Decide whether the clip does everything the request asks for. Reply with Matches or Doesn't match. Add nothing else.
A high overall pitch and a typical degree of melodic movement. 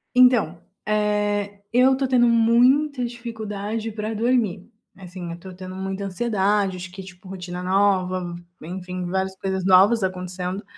Matches